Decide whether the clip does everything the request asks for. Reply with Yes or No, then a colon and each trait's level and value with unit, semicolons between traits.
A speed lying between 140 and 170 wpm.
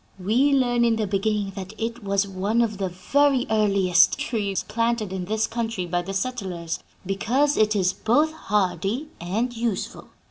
Yes: average, 165 wpm